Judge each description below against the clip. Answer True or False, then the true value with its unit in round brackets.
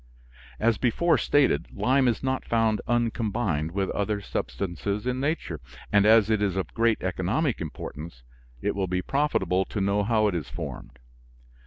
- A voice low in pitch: True (105 Hz)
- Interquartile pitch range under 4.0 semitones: False (4.5 semitones)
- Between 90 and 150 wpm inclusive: False (165 wpm)